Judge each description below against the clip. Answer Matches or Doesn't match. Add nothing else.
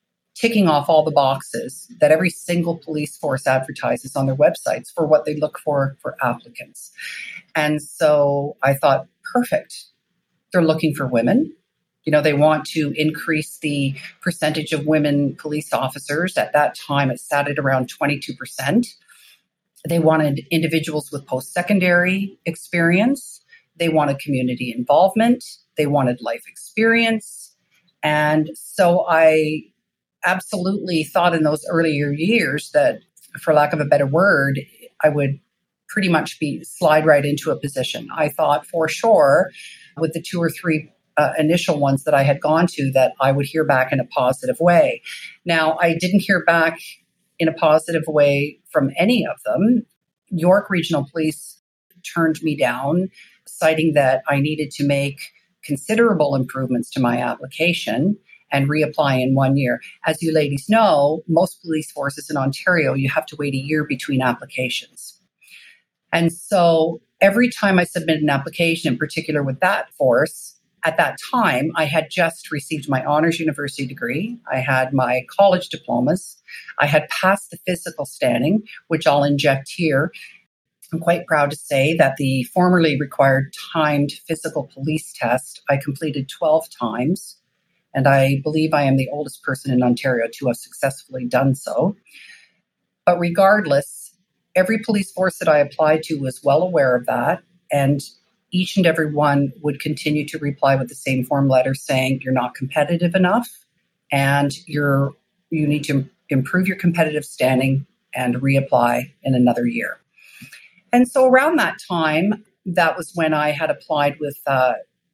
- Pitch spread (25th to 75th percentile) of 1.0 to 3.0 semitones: Doesn't match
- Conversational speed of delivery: Matches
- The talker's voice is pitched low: Doesn't match